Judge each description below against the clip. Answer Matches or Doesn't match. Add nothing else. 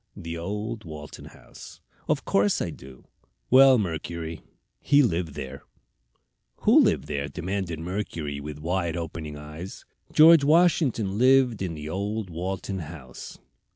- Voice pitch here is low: Matches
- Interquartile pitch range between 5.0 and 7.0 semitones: Matches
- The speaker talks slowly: Matches